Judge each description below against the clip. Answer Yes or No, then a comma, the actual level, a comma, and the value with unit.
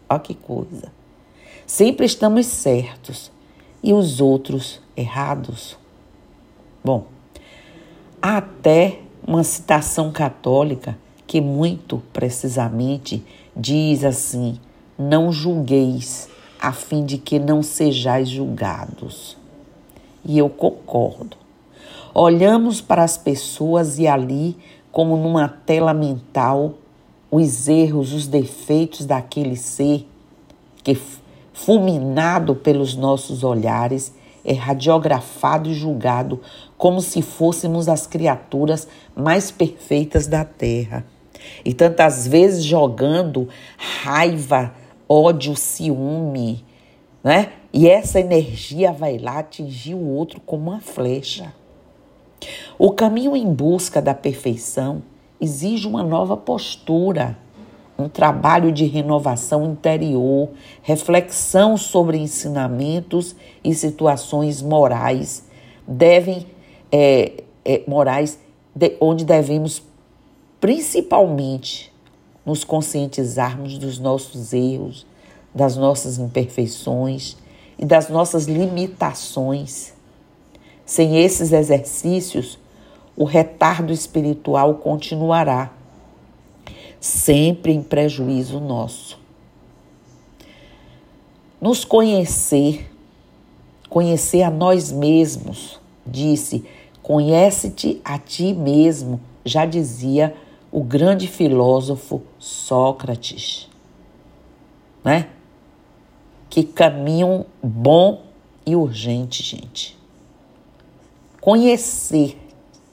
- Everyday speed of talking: No, slow, 85 wpm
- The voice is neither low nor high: Yes, medium, 150 Hz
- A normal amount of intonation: Yes, average, 3.7 semitones